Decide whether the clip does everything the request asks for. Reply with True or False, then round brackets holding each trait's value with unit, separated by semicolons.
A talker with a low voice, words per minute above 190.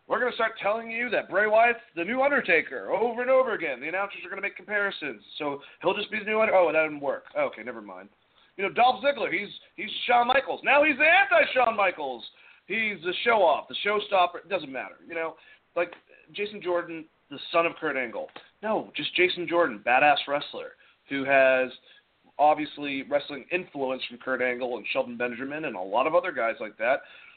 False (185 Hz; 200 wpm)